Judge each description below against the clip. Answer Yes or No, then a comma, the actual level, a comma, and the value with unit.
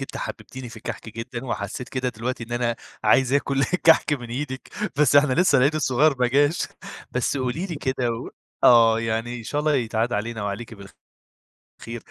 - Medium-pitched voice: No, low, 125 Hz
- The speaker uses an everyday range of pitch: Yes, average, 3.3 semitones